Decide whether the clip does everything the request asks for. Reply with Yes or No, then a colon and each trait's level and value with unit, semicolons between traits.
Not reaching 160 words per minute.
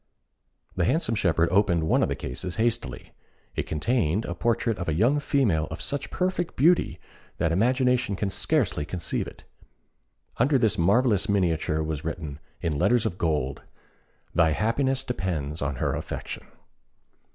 Yes: average, 150 wpm